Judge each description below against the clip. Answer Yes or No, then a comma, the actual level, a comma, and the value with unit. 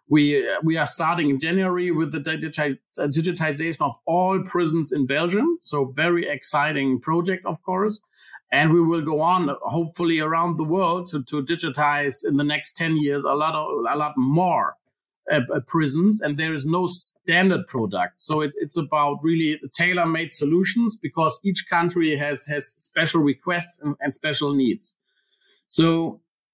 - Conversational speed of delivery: Yes, average, 160 wpm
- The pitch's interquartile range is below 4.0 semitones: Yes, average, 2.9 semitones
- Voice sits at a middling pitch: Yes, medium, 160 Hz